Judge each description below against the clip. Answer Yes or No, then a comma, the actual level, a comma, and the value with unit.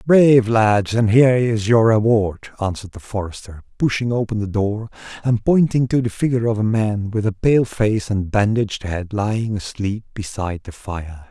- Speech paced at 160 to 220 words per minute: Yes, average, 180 wpm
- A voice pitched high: No, low, 110 Hz